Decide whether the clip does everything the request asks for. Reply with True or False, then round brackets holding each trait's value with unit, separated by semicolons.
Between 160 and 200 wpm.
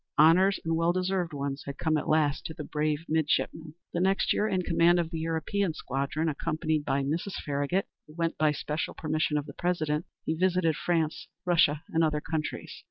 True (190 wpm)